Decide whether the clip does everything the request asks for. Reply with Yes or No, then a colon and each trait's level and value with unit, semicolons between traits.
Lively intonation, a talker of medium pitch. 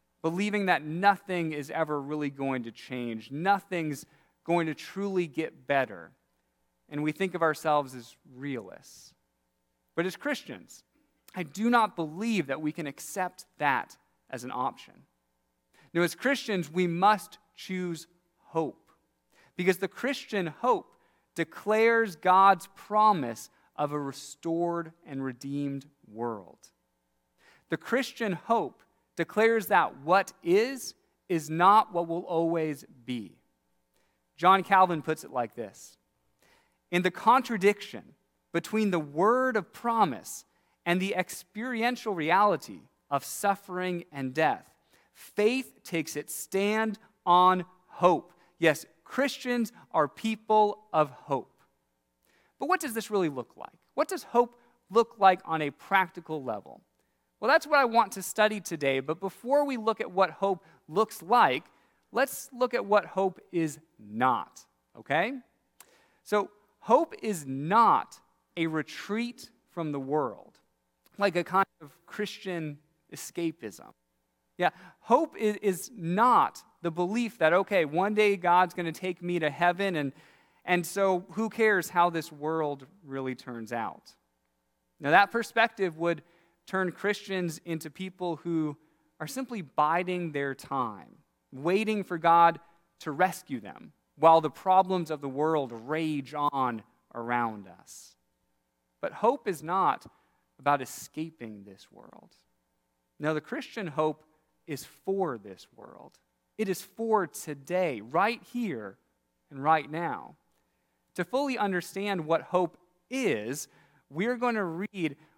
Yes: wide, 5.7 semitones; medium, 170 Hz